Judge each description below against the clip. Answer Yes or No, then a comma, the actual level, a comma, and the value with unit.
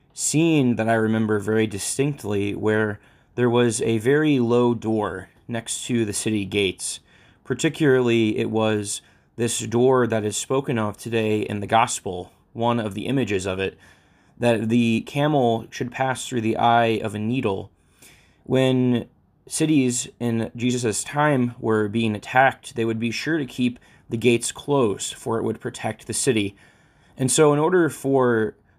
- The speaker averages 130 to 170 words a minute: Yes, average, 160 wpm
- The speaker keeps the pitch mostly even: No, average, 3.1 semitones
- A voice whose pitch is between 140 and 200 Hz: No, low, 115 Hz